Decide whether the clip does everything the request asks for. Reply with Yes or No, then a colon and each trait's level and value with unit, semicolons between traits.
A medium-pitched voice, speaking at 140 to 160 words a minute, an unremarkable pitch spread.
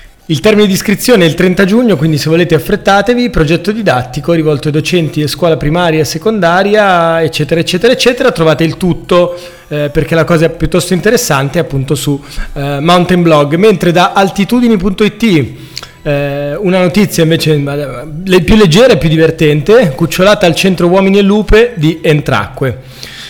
Yes: medium, 170 Hz; average, 155 wpm; average, 4.3 semitones